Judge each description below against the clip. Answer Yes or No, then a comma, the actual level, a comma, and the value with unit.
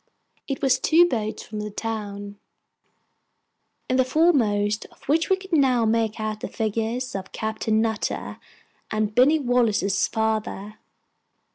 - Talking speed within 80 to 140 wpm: Yes, slow, 135 wpm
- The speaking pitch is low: No, high, 220 Hz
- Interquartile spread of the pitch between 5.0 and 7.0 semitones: No, average, 3.3 semitones